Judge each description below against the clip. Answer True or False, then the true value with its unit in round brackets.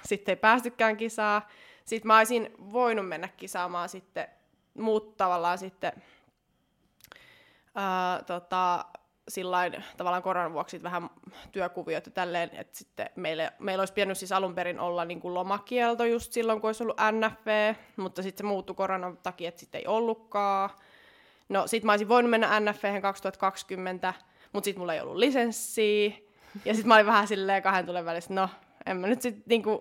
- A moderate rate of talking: False (165 wpm)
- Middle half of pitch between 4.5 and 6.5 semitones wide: False (3.1 semitones)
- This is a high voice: True (195 Hz)